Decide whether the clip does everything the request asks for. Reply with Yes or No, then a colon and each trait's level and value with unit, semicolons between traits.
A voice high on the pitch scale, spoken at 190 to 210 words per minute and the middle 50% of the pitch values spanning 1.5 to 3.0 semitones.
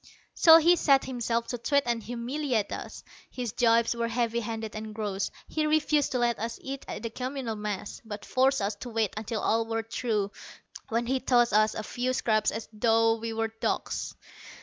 Yes: high, 230 Hz; average, 195 wpm; narrow, 2.5 semitones